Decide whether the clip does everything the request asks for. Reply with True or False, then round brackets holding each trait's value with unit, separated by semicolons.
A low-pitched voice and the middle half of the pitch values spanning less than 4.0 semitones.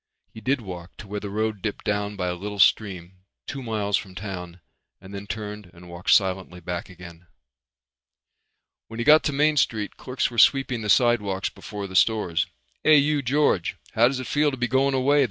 False (105 Hz; 5.2 semitones)